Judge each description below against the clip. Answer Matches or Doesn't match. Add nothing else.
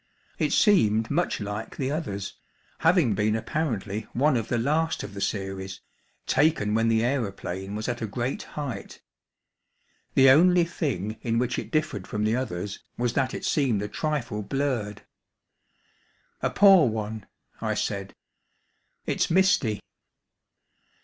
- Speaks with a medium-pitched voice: Doesn't match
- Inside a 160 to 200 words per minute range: Doesn't match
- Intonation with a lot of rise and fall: Matches